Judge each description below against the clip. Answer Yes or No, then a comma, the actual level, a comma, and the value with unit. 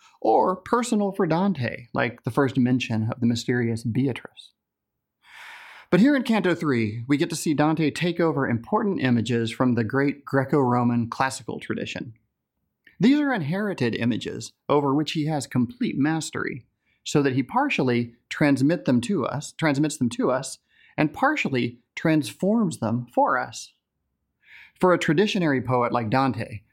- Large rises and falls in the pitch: Yes, wide, 6.2 semitones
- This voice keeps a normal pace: Yes, average, 150 wpm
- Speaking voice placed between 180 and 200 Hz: No, medium, 140 Hz